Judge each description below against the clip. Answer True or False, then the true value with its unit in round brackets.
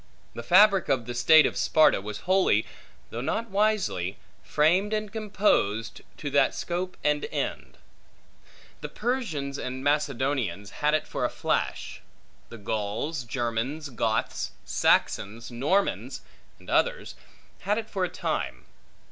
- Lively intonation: True (8.6 semitones)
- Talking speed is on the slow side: True (130 wpm)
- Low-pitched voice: False (145 Hz)